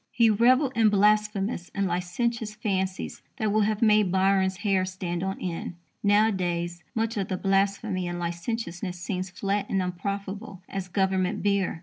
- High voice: Yes, high, 195 Hz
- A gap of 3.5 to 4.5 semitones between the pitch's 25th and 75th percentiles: No, narrow, 2.5 semitones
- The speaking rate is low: No, average, 150 wpm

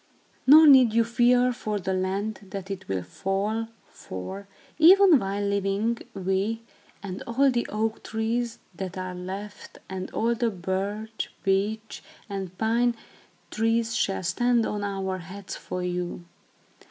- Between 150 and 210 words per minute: No, average, 140 wpm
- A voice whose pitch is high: Yes, high, 205 Hz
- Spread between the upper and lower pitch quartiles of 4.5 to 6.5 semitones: No, average, 3.3 semitones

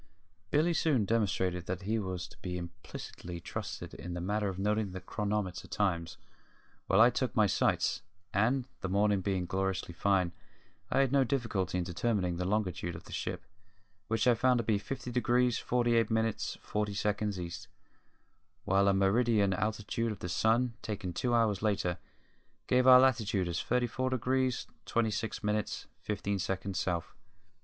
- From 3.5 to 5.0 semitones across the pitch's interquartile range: Yes, average, 4.0 semitones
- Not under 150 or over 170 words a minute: Yes, average, 160 wpm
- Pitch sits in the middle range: No, low, 105 Hz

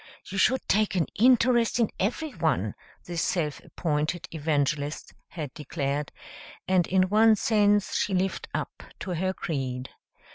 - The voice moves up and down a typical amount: No, wide, 5.7 semitones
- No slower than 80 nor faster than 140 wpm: Yes, slow, 135 wpm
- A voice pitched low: No, medium, 180 Hz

